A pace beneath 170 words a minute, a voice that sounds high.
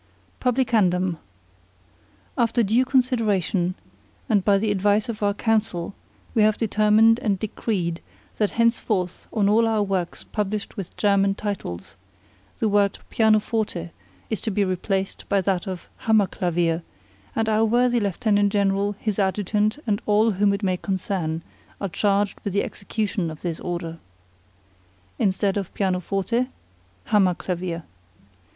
Yes: slow, 135 wpm; high, 200 Hz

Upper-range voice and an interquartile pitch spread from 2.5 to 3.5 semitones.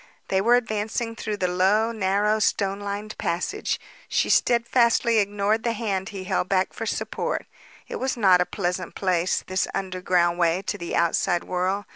Yes: high, 200 Hz; average, 3.0 semitones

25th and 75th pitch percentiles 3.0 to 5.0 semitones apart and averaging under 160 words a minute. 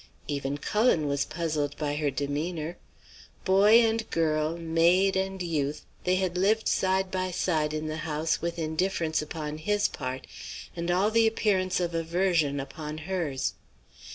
Yes: average, 3.7 semitones; average, 150 wpm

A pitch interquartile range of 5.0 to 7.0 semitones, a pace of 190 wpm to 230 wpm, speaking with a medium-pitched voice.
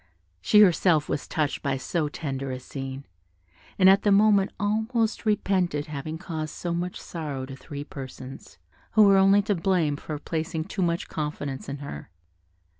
No: wide, 5.4 semitones; average, 165 wpm; medium, 160 Hz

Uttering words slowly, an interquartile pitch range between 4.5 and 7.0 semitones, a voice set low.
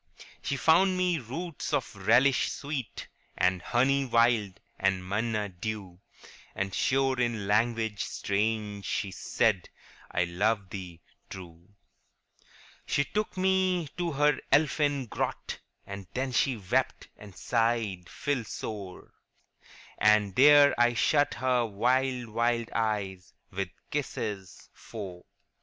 Yes: slow, 125 wpm; wide, 5.4 semitones; low, 115 Hz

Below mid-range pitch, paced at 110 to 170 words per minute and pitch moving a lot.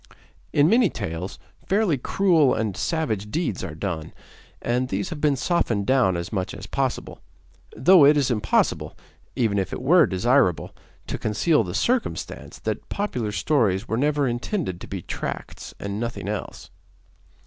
Yes: low, 120 Hz; average, 155 wpm; wide, 7.2 semitones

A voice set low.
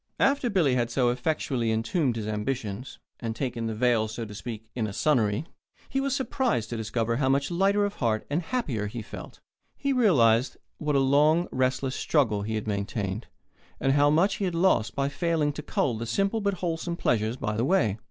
Yes: low, 130 Hz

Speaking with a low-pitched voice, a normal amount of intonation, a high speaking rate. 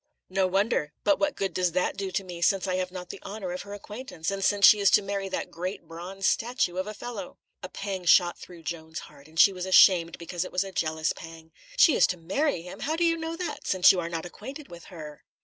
No: medium, 185 Hz; average, 3.0 semitones; fast, 255 wpm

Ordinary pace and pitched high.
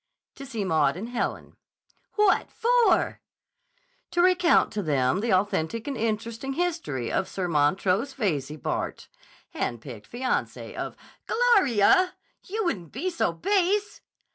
No: slow, 130 wpm; high, 230 Hz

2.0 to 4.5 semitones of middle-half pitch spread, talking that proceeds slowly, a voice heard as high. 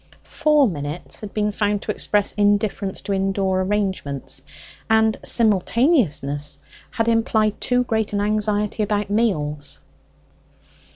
Yes: narrow, 2.5 semitones; slow, 115 wpm; high, 205 Hz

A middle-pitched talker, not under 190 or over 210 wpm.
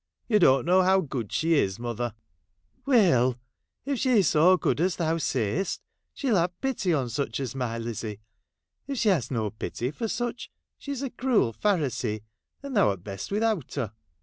Yes: medium, 160 Hz; average, 200 wpm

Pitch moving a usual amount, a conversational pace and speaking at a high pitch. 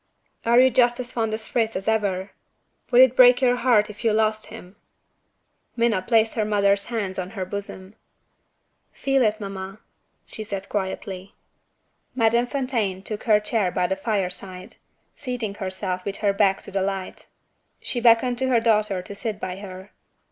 Yes: average, 3.4 semitones; average, 170 wpm; high, 210 Hz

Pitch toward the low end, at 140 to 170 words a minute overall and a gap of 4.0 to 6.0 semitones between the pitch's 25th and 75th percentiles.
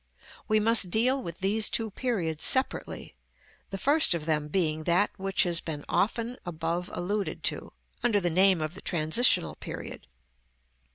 No: high, 190 Hz; average, 155 wpm; average, 5.1 semitones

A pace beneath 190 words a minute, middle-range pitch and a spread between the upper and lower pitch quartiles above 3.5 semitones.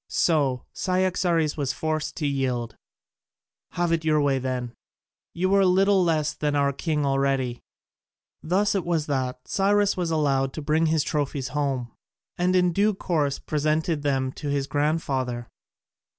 Yes: average, 150 wpm; medium, 150 Hz; average, 4.0 semitones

